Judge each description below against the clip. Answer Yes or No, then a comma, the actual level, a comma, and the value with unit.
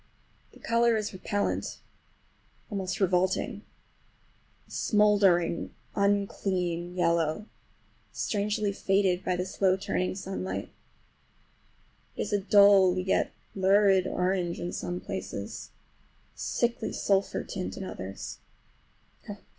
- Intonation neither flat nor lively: No, narrow, 1.9 semitones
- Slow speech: Yes, slow, 100 wpm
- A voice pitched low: No, high, 190 Hz